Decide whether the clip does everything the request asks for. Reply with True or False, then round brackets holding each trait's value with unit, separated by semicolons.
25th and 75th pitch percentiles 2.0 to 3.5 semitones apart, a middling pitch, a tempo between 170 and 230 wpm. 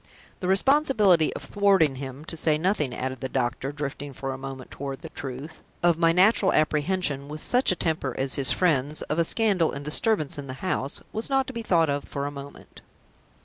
False (5.1 semitones; 155 Hz; 205 wpm)